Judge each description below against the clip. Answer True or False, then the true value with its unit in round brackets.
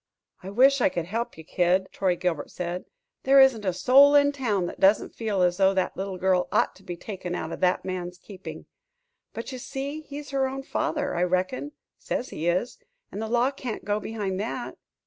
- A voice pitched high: True (200 Hz)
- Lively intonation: True (6.4 semitones)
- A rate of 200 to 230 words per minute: True (205 wpm)